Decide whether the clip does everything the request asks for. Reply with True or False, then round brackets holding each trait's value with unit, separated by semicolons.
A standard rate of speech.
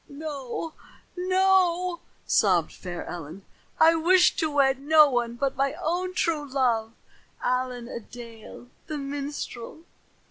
False (120 wpm)